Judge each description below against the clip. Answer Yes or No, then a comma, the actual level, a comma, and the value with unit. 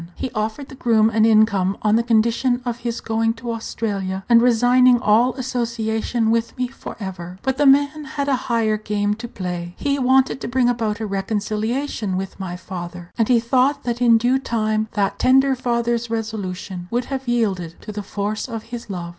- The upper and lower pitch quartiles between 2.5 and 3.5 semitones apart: Yes, average, 2.8 semitones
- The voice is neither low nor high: No, high, 225 Hz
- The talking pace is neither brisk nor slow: Yes, average, 190 wpm